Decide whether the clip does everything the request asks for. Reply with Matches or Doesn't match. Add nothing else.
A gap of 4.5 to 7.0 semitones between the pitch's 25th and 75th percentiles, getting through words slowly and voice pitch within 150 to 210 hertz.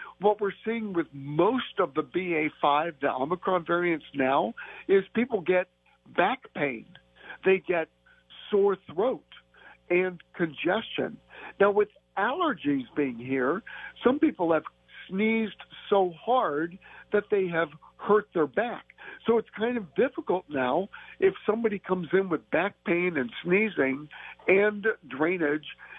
Matches